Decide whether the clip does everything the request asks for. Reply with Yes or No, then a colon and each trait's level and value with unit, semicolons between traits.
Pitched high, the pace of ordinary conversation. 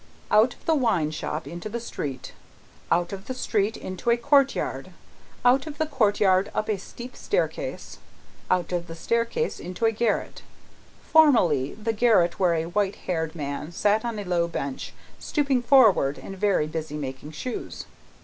Yes: high, 205 Hz; average, 165 wpm